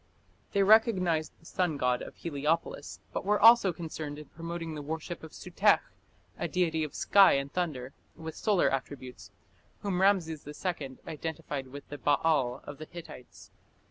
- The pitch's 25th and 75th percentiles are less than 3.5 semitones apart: No, average, 3.8 semitones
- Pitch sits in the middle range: Yes, medium, 160 Hz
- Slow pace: No, average, 155 wpm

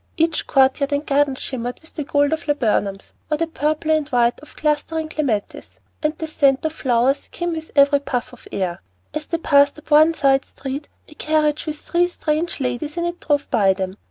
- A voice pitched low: No, very high, 295 Hz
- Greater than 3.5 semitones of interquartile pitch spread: No, average, 2.9 semitones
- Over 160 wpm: Yes, fast, 205 wpm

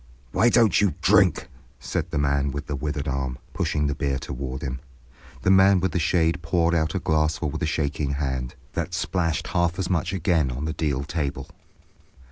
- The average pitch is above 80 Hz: No, very low, 75 Hz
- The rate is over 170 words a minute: Yes, average, 190 wpm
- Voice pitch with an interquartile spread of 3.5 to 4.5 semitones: Yes, average, 3.8 semitones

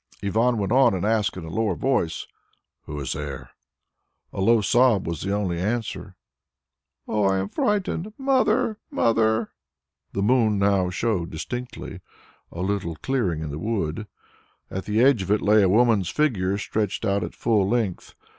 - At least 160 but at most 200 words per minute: Yes, average, 165 wpm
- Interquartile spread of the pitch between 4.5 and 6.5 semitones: No, average, 4.0 semitones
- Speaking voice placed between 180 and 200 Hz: No, low, 105 Hz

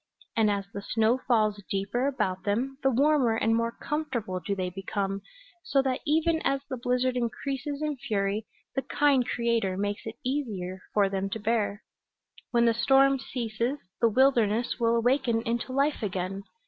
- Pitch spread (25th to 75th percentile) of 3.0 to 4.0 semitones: No, average, 4.7 semitones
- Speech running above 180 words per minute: No, average, 165 wpm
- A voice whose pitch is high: Yes, high, 230 Hz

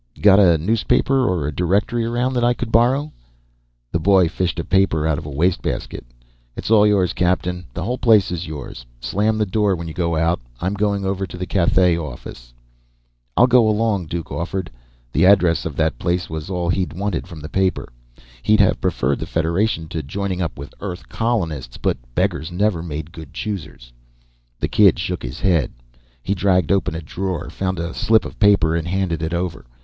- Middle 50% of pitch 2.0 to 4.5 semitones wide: Yes, average, 3.7 semitones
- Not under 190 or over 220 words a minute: Yes, average, 195 wpm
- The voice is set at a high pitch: No, very low, 90 Hz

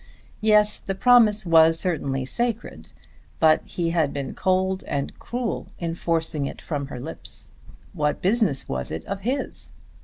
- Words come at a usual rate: Yes, average, 150 wpm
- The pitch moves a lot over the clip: Yes, wide, 6.0 semitones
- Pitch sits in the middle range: Yes, medium, 170 Hz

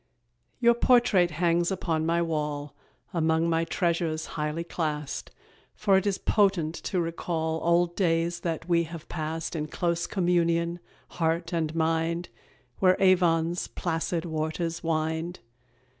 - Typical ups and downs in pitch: No, narrow, 1.4 semitones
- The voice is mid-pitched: Yes, medium, 170 Hz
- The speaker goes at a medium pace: No, slow, 130 wpm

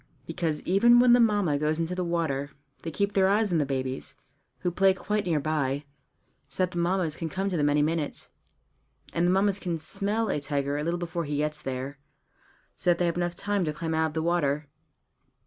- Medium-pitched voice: Yes, medium, 170 Hz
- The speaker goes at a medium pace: No, fast, 215 wpm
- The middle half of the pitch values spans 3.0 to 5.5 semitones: Yes, average, 4.0 semitones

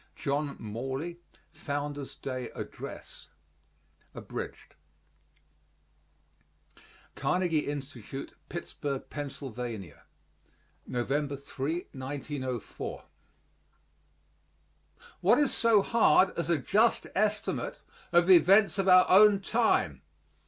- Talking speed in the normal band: No, slow, 80 wpm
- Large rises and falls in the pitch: Yes, wide, 5.7 semitones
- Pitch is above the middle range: No, medium, 150 Hz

